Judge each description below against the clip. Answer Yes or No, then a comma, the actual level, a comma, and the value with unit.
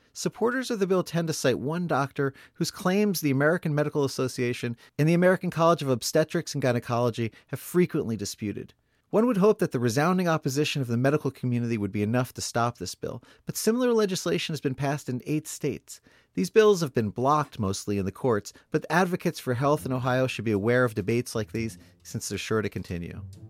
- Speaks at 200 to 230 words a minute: Yes, fast, 205 wpm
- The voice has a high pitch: No, low, 135 Hz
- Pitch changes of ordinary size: No, wide, 6.1 semitones